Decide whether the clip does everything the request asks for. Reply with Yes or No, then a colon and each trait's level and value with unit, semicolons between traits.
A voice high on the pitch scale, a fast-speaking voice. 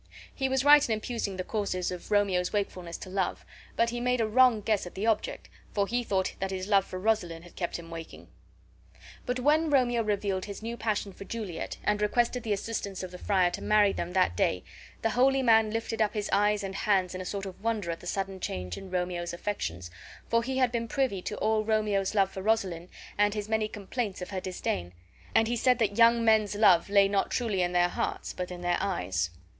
Yes: high, 205 Hz; fast, 225 wpm